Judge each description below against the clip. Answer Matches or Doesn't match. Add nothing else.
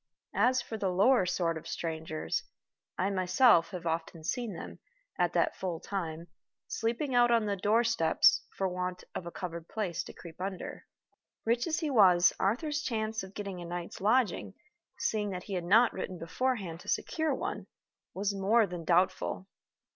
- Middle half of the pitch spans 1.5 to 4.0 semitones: Doesn't match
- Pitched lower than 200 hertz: Matches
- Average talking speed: Matches